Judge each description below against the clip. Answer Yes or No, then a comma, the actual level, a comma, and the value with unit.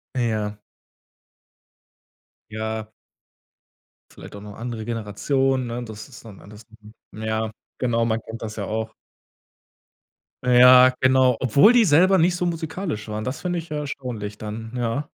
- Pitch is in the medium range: No, low, 120 Hz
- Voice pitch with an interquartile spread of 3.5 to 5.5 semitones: Yes, average, 3.8 semitones